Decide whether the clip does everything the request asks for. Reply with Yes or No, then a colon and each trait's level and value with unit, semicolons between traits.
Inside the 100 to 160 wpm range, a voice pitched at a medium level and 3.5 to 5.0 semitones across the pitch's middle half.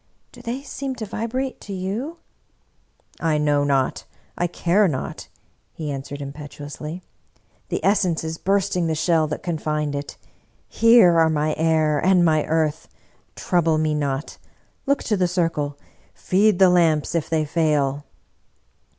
Yes: average, 155 wpm; medium, 160 Hz; average, 3.9 semitones